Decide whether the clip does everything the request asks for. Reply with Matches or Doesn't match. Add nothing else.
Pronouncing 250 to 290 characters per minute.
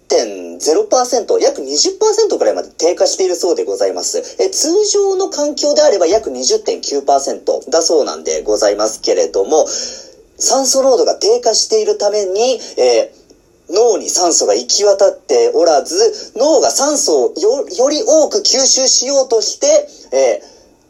Matches